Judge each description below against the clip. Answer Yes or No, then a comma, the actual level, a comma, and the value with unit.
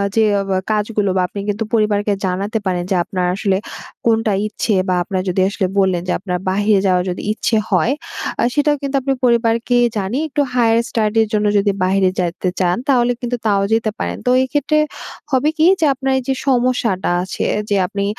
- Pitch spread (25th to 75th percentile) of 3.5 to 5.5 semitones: Yes, average, 4.1 semitones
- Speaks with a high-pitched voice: Yes, high, 215 Hz